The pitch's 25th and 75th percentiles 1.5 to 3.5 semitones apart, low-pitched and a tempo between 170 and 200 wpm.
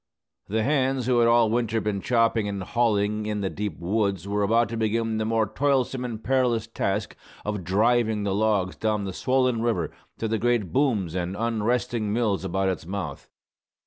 Yes: average, 2.8 semitones; low, 110 Hz; average, 180 wpm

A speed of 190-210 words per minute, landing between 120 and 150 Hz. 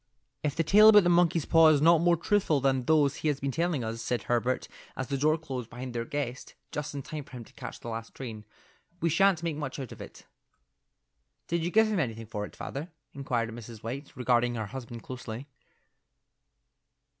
Yes: fast, 205 wpm; low, 135 Hz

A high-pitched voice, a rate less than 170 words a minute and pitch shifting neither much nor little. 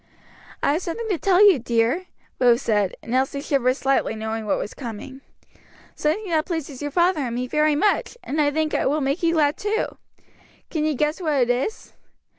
No: very high, 290 Hz; average, 195 wpm; average, 4.8 semitones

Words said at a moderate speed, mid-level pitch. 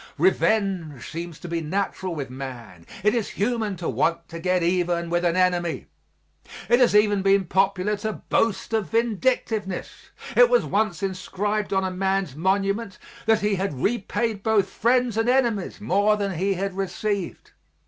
No: average, 160 wpm; high, 195 Hz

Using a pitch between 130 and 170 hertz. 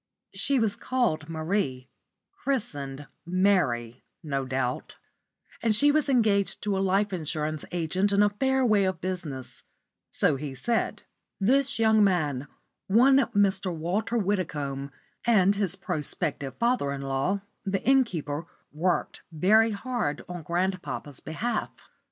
No: medium, 185 Hz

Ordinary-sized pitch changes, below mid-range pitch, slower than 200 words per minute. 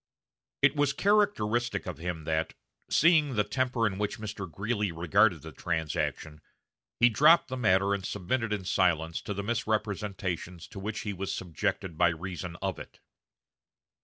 Yes: average, 4.9 semitones; low, 100 Hz; average, 155 wpm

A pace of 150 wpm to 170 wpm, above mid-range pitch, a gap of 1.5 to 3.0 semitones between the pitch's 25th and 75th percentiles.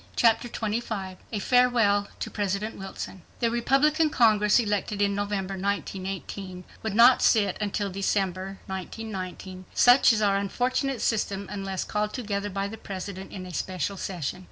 No: slow, 135 wpm; high, 205 Hz; narrow, 2.6 semitones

